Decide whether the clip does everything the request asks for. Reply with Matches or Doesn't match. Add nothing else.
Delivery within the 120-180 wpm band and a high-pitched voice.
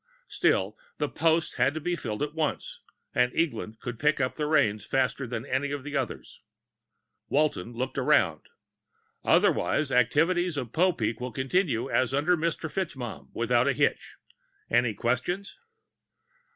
Doesn't match